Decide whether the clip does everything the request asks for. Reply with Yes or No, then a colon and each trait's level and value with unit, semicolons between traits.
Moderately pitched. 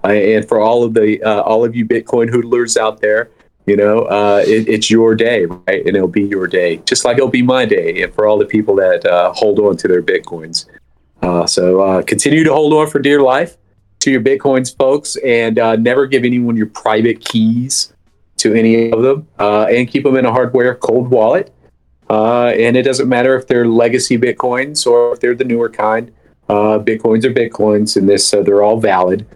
No: low, 115 Hz